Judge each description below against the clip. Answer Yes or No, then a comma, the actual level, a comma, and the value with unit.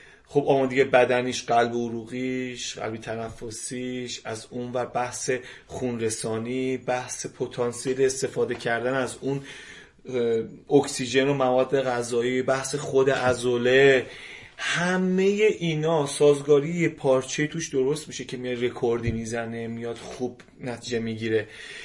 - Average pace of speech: Yes, average, 115 wpm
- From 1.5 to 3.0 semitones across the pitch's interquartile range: Yes, narrow, 2.4 semitones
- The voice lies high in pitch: No, low, 125 Hz